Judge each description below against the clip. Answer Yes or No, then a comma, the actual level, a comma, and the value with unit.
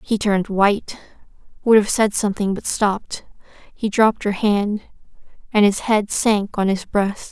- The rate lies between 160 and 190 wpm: Yes, average, 165 wpm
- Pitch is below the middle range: No, high, 205 Hz